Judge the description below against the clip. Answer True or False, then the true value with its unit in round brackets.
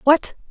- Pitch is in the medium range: False (300 Hz)